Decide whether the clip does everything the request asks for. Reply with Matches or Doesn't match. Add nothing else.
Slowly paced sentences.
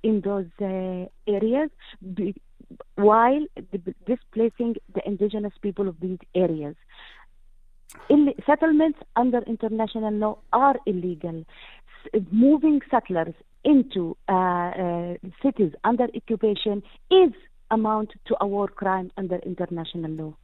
Matches